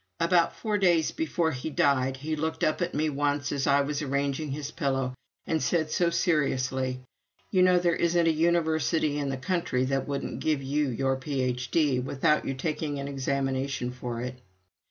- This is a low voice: No, medium, 145 Hz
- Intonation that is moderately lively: Yes, average, 3.2 semitones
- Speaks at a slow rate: No, average, 175 wpm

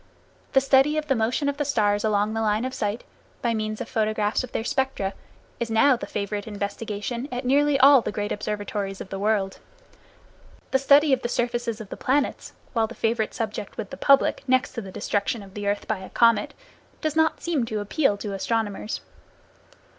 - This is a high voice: Yes, high, 225 Hz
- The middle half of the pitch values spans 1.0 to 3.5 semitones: No, average, 4.2 semitones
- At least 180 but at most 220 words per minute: Yes, average, 200 wpm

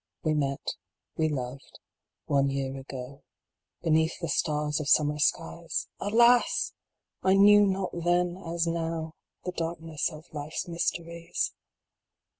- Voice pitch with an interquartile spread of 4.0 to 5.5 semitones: No, average, 2.8 semitones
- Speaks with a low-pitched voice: No, medium, 165 Hz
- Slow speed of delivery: Yes, slow, 125 wpm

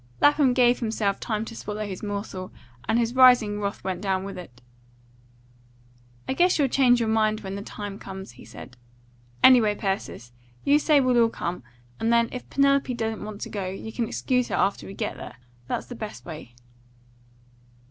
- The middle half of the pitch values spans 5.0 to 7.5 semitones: No, average, 3.9 semitones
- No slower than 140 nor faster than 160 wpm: No, average, 185 wpm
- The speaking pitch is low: No, high, 220 Hz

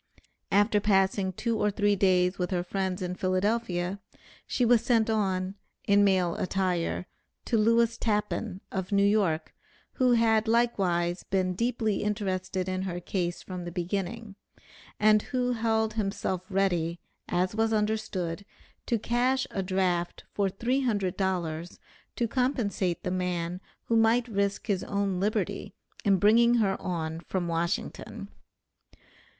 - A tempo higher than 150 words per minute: No, average, 140 wpm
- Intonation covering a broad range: No, average, 3.4 semitones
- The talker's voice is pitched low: No, high, 195 Hz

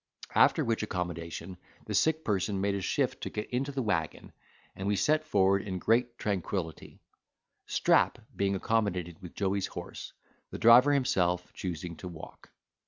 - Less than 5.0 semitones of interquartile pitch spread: Yes, average, 4.2 semitones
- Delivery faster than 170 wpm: No, average, 155 wpm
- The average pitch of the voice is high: No, low, 100 Hz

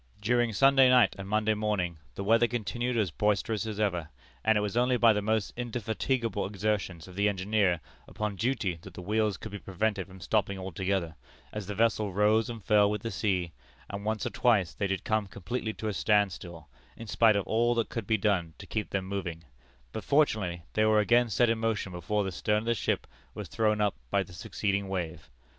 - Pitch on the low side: Yes, low, 105 Hz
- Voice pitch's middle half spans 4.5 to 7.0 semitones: No, narrow, 2.5 semitones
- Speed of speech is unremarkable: No, fast, 210 wpm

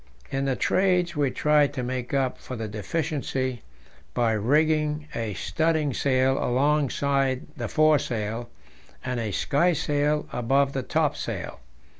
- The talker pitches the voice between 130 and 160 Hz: Yes, low, 135 Hz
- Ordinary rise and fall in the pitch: Yes, average, 3.4 semitones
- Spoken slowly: Yes, slow, 130 wpm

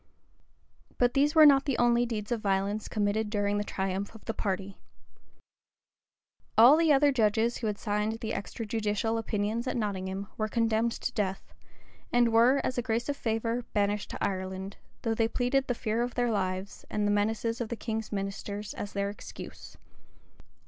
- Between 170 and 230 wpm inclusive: Yes, average, 175 wpm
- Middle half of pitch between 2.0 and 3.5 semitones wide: Yes, average, 2.7 semitones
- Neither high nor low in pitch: No, high, 220 Hz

